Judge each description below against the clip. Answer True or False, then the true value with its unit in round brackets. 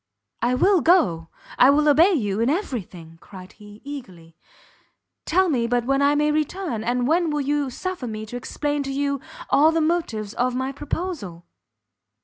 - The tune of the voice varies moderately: False (5.8 semitones)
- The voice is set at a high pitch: True (275 Hz)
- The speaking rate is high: False (175 wpm)